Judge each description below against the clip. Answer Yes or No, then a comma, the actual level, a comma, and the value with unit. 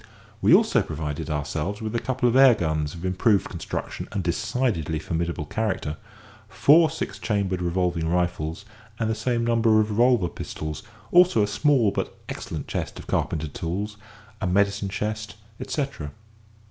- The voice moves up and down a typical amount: No, wide, 5.7 semitones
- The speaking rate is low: No, average, 150 wpm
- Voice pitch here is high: No, low, 100 Hz